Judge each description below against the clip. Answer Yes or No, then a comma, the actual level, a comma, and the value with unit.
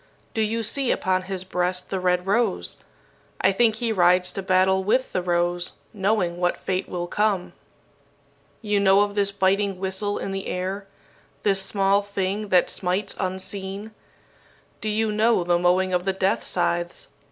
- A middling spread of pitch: No, narrow, 2.0 semitones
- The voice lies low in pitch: No, high, 190 Hz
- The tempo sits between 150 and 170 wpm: Yes, average, 165 wpm